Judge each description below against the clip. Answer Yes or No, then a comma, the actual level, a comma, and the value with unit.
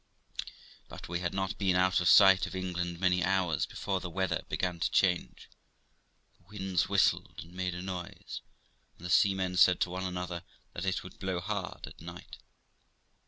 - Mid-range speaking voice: No, very low, 90 Hz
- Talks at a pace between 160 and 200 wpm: Yes, average, 175 wpm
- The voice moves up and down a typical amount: No, narrow, 1.2 semitones